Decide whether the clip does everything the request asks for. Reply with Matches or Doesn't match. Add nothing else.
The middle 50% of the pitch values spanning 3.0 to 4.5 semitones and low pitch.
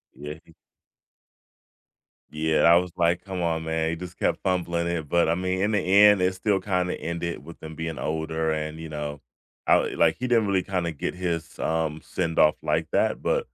Doesn't match